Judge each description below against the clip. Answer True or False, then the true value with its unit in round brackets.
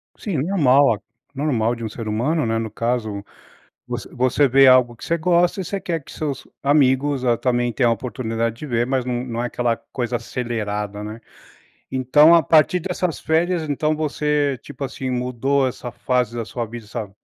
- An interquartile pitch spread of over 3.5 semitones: True (4.1 semitones)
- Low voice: True (125 Hz)